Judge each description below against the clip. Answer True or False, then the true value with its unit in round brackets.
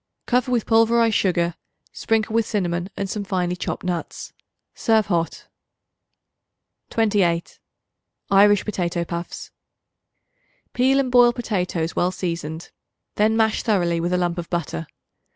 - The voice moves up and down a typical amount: True (4.4 semitones)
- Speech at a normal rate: False (125 wpm)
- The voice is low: False (190 Hz)